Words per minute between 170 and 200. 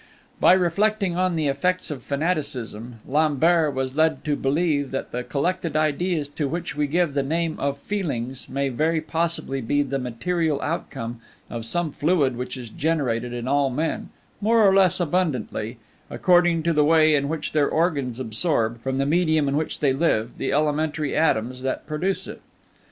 Yes: average, 175 wpm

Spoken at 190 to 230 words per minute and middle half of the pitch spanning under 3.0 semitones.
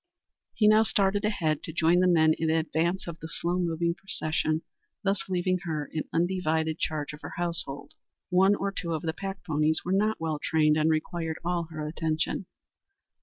No: average, 180 wpm; narrow, 2.6 semitones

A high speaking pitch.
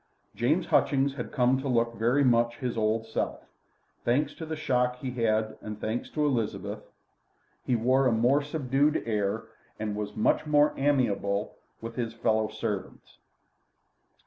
No: low, 120 Hz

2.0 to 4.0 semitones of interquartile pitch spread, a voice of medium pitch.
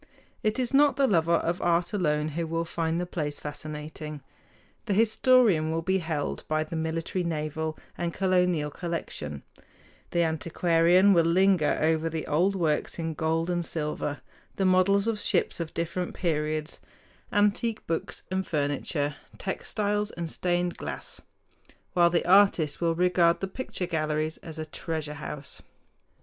Yes: average, 2.9 semitones; medium, 170 Hz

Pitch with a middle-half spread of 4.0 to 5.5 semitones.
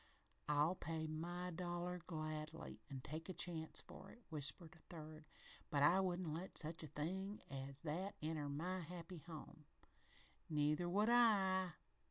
No: average, 2.8 semitones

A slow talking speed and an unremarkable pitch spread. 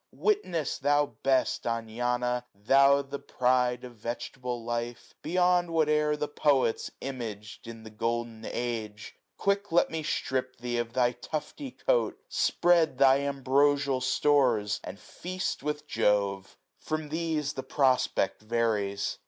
Yes: slow, 130 wpm; average, 4.2 semitones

